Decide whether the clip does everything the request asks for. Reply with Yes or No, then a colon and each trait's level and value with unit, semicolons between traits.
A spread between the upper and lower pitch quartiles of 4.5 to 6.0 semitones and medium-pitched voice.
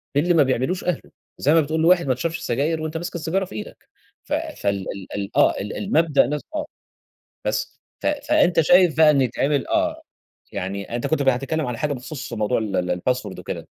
Yes: wide, 5.5 semitones; medium, 150 Hz